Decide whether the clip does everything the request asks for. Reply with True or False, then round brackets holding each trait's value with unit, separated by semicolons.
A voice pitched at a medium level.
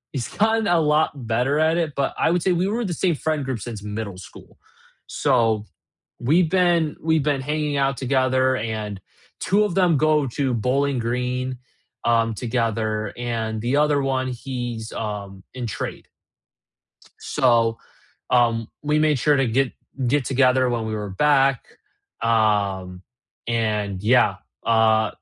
False (125 Hz)